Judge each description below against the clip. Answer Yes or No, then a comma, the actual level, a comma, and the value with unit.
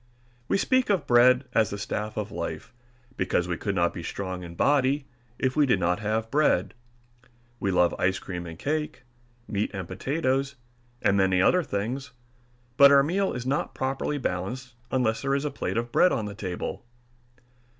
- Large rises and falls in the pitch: Yes, wide, 6.5 semitones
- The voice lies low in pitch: Yes, low, 115 Hz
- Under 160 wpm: No, average, 180 wpm